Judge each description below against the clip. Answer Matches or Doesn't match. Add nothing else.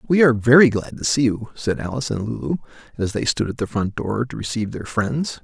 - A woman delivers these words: Doesn't match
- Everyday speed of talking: Doesn't match